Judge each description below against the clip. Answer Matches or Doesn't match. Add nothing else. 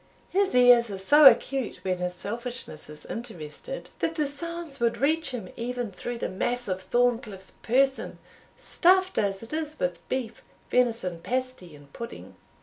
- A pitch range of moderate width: Doesn't match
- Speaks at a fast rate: Doesn't match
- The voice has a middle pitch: Doesn't match